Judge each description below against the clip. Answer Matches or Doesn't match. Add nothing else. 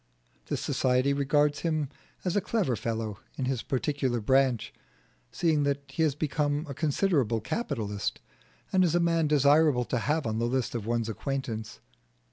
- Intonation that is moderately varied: Matches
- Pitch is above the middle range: Doesn't match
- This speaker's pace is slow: Doesn't match